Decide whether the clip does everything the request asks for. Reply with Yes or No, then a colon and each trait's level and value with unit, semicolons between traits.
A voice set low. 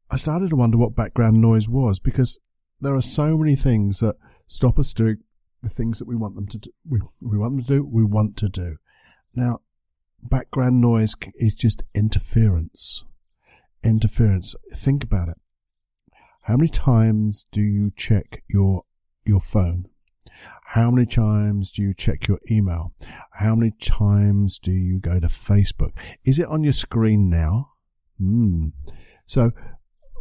Yes: low, 110 Hz